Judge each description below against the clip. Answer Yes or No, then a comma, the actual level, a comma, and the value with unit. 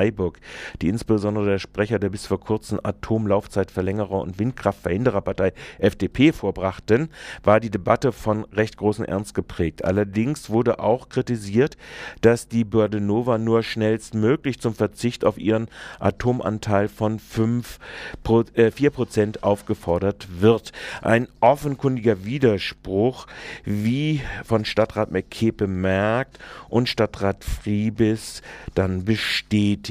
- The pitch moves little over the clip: Yes, narrow, 2.3 semitones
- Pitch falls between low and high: No, low, 110 Hz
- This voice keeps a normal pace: No, slow, 105 wpm